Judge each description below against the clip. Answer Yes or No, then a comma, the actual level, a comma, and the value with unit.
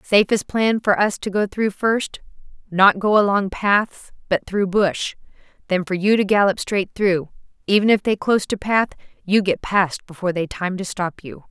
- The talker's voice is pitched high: Yes, high, 195 Hz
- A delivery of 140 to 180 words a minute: No, average, 195 wpm